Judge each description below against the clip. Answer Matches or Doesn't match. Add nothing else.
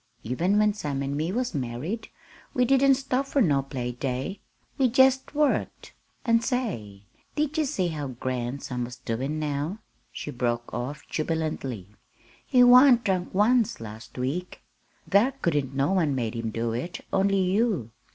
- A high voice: Doesn't match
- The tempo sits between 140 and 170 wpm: Matches